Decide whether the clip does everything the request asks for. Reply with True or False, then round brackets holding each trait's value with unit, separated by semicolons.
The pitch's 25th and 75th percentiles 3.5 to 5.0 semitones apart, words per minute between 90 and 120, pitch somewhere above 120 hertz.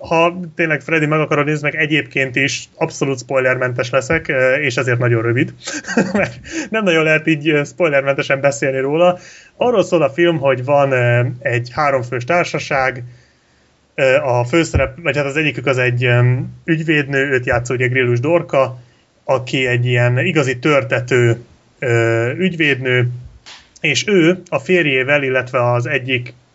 False (4.1 semitones; 135 wpm; 140 Hz)